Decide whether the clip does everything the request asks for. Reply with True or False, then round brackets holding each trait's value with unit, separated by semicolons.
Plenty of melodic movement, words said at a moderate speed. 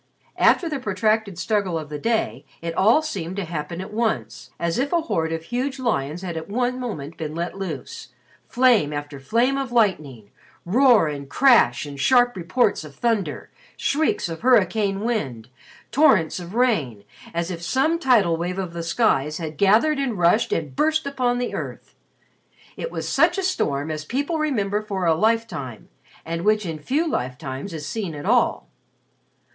True (7.3 semitones; 175 wpm)